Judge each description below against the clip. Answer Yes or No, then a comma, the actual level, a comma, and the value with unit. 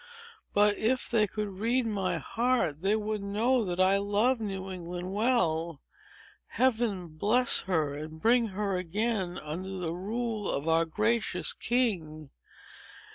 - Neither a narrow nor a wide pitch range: Yes, average, 4.4 semitones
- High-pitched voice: Yes, high, 200 Hz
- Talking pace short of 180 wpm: Yes, slow, 135 wpm